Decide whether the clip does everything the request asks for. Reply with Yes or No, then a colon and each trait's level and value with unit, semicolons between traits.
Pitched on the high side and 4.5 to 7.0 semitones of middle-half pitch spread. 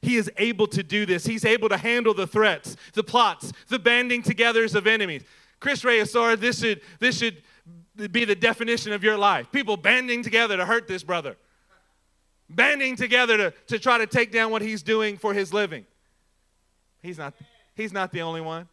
No: high, 215 Hz; average, 4.0 semitones